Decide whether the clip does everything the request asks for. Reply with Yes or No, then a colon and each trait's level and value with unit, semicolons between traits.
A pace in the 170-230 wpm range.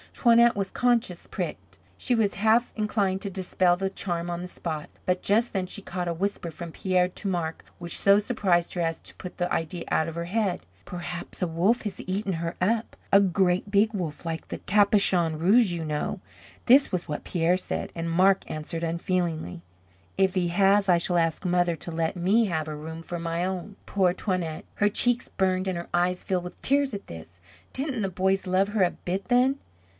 Yes: fast, 205 wpm